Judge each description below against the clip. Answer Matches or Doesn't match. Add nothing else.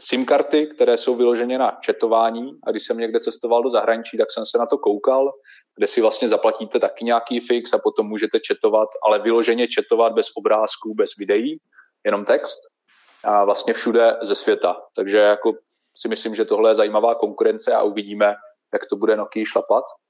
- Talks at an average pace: Doesn't match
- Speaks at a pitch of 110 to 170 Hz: Matches